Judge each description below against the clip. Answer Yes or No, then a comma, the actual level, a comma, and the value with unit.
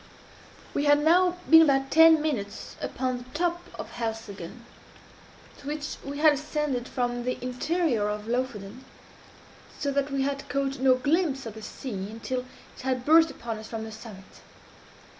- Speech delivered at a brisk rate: No, average, 160 wpm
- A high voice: Yes, very high, 265 Hz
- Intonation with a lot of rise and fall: No, average, 4.4 semitones